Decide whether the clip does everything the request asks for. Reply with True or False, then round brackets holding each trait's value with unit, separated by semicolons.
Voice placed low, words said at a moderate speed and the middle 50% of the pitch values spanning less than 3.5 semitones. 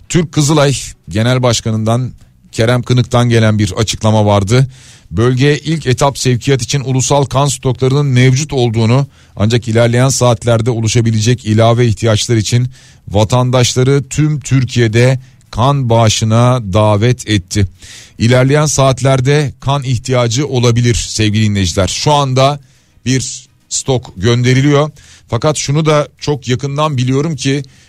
True (125 Hz; 115 wpm; 3.0 semitones)